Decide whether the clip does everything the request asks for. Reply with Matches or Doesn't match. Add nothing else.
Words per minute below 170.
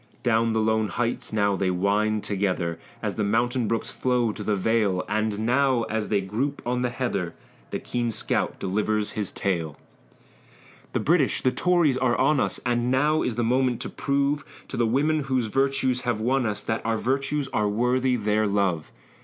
Doesn't match